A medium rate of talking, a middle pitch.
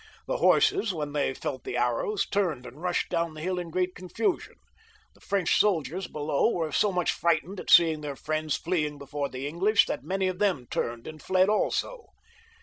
Yes: average, 190 wpm; medium, 170 Hz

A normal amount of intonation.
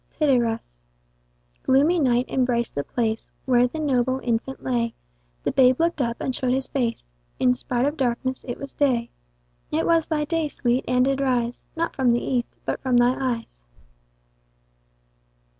No: narrow, 2.3 semitones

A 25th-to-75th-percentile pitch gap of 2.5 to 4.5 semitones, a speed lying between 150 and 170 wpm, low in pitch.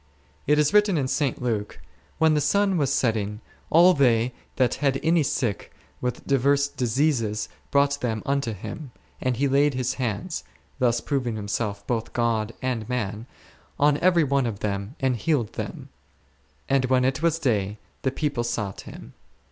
Yes: average, 4.0 semitones; average, 165 wpm; low, 130 Hz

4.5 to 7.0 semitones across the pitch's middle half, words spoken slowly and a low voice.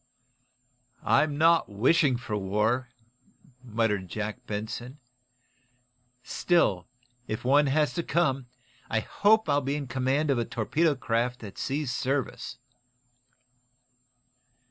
Yes: average, 4.9 semitones; slow, 110 wpm; low, 130 Hz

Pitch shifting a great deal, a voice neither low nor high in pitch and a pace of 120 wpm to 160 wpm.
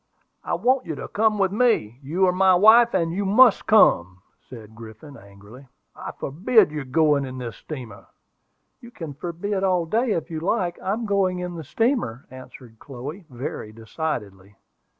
No: wide, 7.9 semitones; medium, 160 Hz; average, 170 wpm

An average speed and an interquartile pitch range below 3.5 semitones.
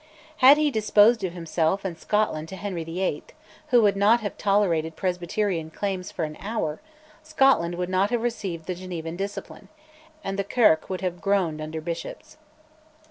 No: average, 165 wpm; average, 3.8 semitones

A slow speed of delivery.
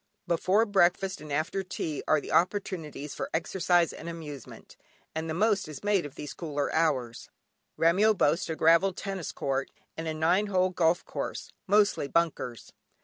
No: average, 160 wpm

